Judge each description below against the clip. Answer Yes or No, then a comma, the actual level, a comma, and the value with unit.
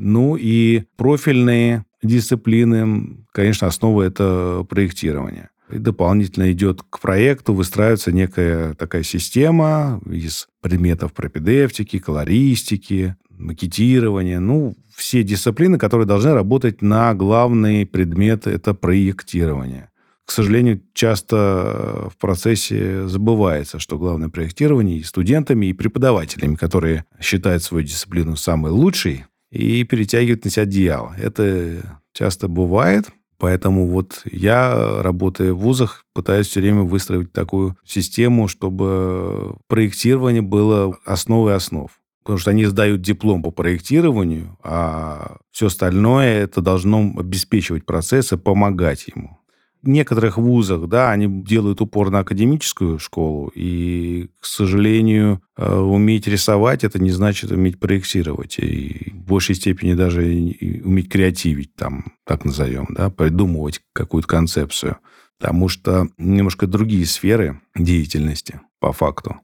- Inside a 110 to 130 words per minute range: Yes, average, 115 wpm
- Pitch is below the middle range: Yes, low, 100 Hz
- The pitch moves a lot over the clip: No, average, 3.9 semitones